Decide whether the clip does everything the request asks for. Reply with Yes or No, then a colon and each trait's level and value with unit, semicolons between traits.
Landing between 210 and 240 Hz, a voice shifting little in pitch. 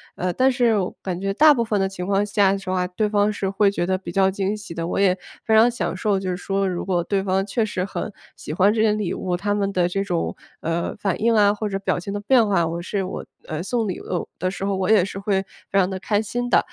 No: high, 195 Hz; narrow, 2.2 semitones